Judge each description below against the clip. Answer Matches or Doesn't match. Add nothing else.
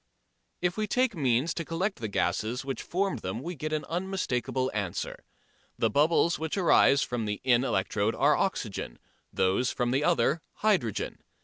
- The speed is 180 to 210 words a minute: Doesn't match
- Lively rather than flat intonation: Matches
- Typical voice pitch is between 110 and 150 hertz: Matches